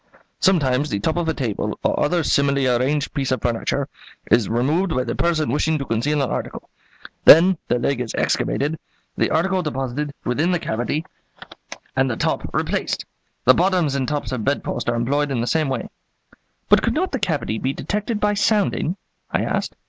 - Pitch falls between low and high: Yes, medium, 145 Hz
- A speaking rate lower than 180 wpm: No, average, 185 wpm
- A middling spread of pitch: Yes, average, 4.5 semitones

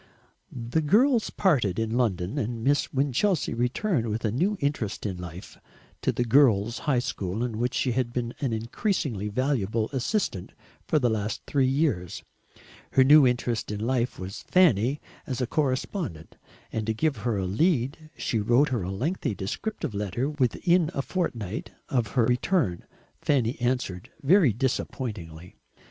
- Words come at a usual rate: Yes, average, 155 wpm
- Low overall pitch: Yes, low, 120 Hz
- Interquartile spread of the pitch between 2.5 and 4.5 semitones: No, average, 5.1 semitones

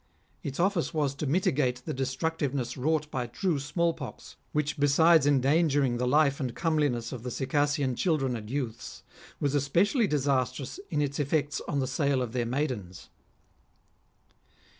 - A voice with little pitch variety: No, average, 3.0 semitones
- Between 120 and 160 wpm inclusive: Yes, average, 150 wpm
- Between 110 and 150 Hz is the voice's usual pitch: Yes, medium, 140 Hz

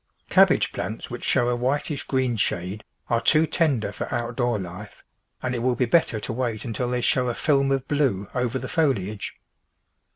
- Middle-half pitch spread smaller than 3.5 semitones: Yes, average, 2.8 semitones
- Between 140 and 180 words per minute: No, average, 190 wpm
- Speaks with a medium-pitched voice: No, low, 125 Hz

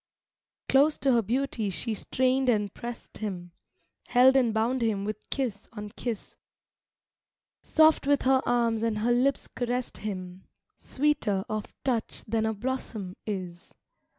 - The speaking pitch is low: No, high, 230 Hz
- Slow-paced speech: No, average, 145 wpm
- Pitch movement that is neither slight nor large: Yes, average, 3.8 semitones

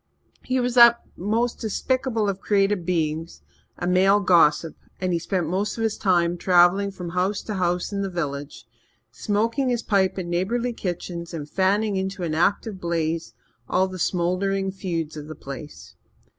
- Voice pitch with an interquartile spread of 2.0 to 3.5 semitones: Yes, average, 3.2 semitones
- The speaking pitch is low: No, medium, 185 Hz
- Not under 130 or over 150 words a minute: No, average, 165 wpm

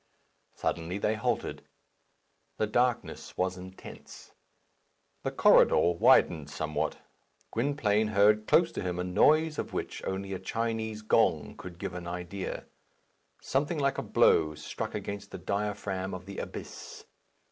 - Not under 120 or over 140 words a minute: Yes, slow, 135 wpm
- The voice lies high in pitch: No, low, 100 Hz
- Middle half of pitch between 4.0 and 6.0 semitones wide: No, average, 3.6 semitones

